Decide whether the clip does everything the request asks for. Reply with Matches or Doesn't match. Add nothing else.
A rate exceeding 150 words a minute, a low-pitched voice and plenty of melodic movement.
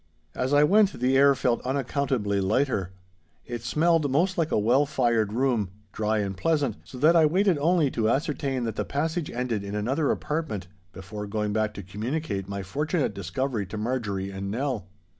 Matches